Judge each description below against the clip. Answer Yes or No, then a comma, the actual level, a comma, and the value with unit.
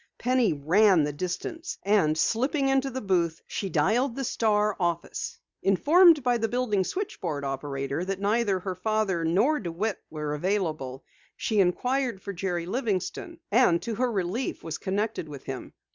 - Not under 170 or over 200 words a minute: No, average, 155 wpm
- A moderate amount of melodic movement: No, wide, 6.1 semitones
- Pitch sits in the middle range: No, high, 195 Hz